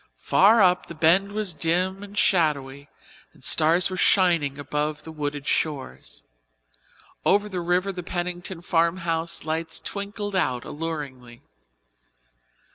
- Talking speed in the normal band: No, slow, 120 wpm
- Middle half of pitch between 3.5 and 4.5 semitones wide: Yes, average, 3.9 semitones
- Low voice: No, medium, 170 Hz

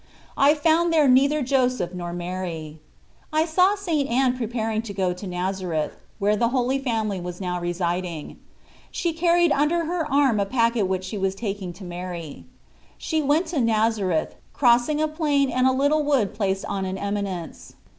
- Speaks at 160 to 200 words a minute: Yes, average, 170 wpm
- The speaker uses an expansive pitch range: Yes, wide, 7.5 semitones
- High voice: Yes, high, 225 Hz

